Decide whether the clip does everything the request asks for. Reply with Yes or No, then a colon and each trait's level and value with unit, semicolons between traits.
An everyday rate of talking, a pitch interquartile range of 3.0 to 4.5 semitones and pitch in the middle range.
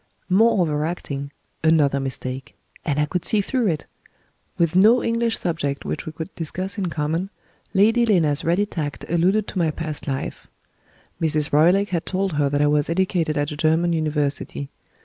Yes: average, 170 wpm; average, 4.2 semitones; medium, 165 Hz